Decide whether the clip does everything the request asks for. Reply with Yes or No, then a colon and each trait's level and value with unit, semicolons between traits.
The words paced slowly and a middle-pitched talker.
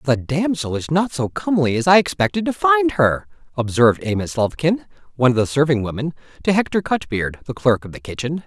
No: average, 200 wpm; medium, 150 Hz